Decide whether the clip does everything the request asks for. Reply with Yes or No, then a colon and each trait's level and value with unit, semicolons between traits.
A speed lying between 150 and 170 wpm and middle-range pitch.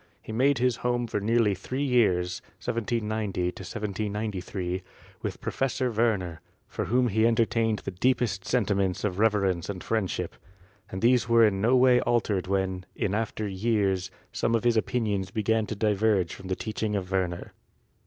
No: average, 160 wpm; low, 105 Hz